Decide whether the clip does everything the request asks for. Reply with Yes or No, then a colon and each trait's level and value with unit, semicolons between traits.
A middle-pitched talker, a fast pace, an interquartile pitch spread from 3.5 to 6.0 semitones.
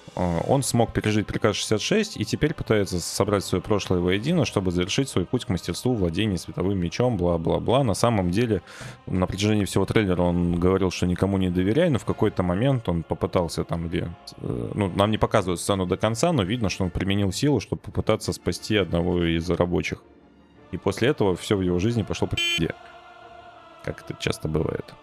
No: low, 100 Hz; fast, 180 wpm; average, 4.2 semitones